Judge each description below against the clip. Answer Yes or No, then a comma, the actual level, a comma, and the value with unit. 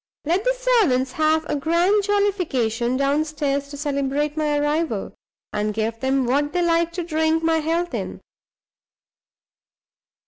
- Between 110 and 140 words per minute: Yes, slow, 135 wpm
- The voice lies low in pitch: No, very high, 300 Hz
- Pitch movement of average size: Yes, average, 3.6 semitones